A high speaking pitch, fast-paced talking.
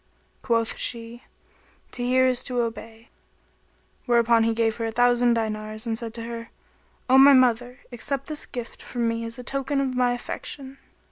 No: high, 240 Hz; average, 175 wpm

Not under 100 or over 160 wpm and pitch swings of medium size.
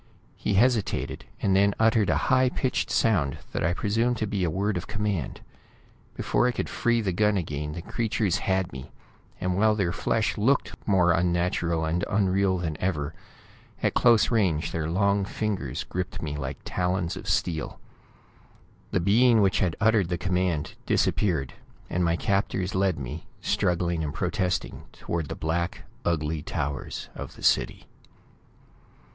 Yes: average, 155 wpm; average, 3.9 semitones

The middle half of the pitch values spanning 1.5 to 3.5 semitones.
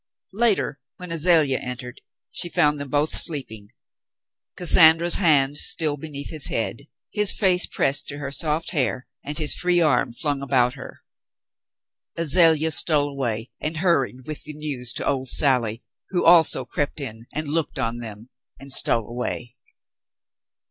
No: average, 4.0 semitones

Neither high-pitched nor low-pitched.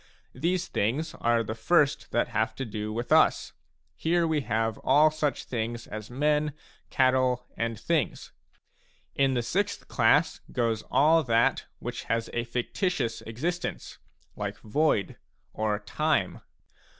No: low, 125 Hz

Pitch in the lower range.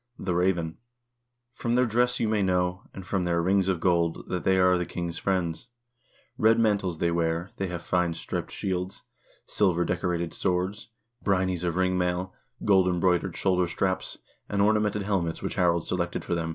Yes: very low, 90 Hz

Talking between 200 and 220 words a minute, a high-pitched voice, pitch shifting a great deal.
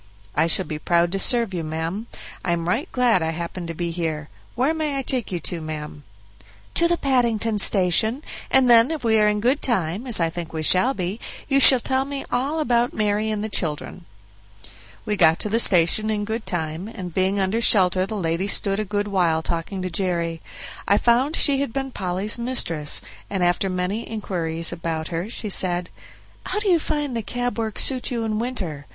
Yes: fast, 205 wpm; high, 205 Hz; wide, 5.7 semitones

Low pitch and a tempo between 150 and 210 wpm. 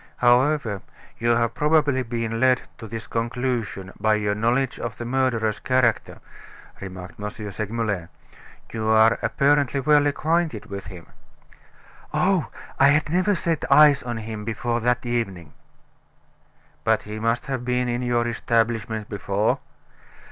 No: low, 120 Hz; slow, 135 wpm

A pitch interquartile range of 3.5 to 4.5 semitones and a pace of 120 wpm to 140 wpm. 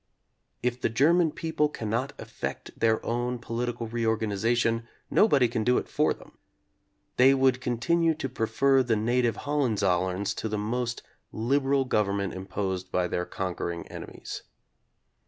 Yes: average, 3.8 semitones; slow, 135 wpm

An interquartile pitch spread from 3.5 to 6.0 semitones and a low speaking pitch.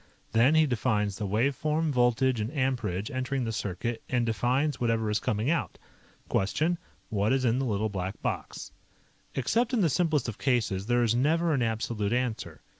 Yes: average, 4.1 semitones; low, 120 Hz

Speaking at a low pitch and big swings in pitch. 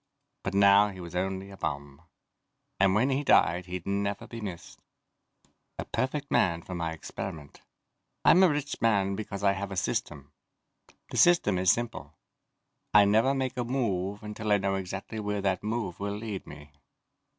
No: low, 100 Hz; average, 3.2 semitones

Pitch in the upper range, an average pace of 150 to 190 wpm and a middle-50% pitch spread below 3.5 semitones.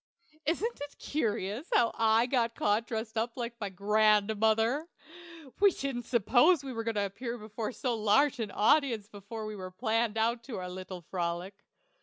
Yes: high, 225 Hz; average, 160 wpm; average, 2.7 semitones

